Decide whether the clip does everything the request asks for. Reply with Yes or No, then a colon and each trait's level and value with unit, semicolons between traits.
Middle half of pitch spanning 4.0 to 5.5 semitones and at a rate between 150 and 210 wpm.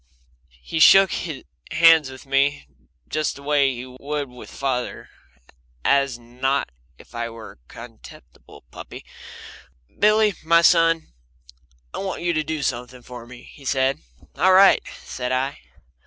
No: average, 4.4 semitones; average, 140 wpm